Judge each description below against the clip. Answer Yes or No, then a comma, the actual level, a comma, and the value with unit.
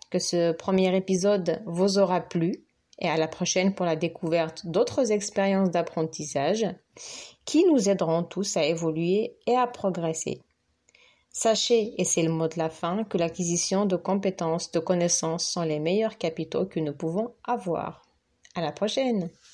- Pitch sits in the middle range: Yes, medium, 180 Hz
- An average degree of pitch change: Yes, average, 3.5 semitones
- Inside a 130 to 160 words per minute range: Yes, average, 155 wpm